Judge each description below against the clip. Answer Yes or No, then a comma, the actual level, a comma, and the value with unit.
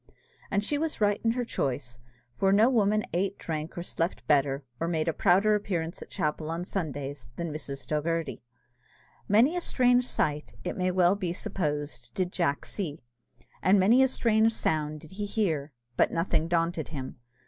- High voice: No, medium, 175 Hz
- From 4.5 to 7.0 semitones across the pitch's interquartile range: Yes, average, 5.2 semitones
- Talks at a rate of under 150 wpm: No, average, 175 wpm